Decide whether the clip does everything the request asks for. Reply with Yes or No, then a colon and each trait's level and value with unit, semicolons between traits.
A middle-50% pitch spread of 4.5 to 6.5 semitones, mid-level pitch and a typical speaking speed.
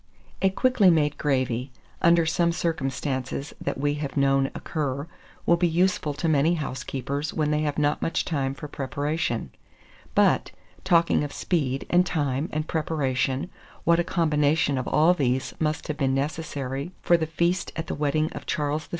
No: average, 3.2 semitones; medium, 150 Hz; average, 165 wpm